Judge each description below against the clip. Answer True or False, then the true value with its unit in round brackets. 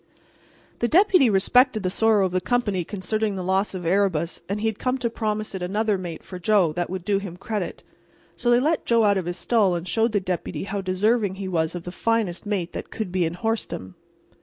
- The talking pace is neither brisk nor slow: False (225 wpm)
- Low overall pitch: False (200 Hz)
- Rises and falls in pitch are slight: False (3.5 semitones)